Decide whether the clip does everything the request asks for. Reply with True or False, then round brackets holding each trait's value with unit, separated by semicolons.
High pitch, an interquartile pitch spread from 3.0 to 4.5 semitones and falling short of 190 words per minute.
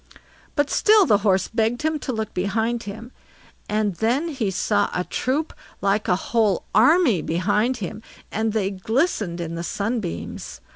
True (220 Hz; 4.0 semitones; 155 wpm)